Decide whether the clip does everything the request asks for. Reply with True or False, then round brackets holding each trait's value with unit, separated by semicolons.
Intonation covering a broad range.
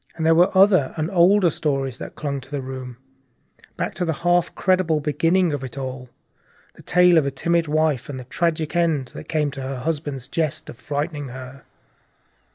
False (4.0 semitones)